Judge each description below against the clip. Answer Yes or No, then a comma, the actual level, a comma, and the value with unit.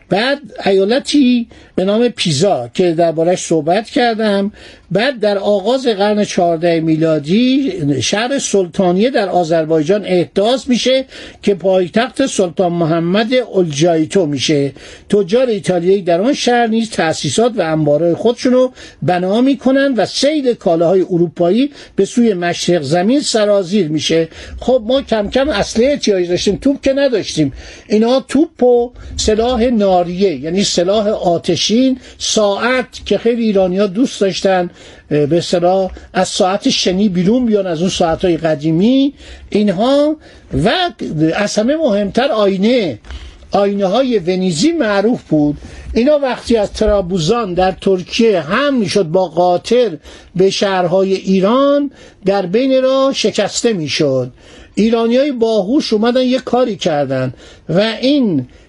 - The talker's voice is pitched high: Yes, high, 205 Hz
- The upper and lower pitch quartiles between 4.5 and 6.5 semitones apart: Yes, average, 5.3 semitones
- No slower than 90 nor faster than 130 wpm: Yes, average, 125 wpm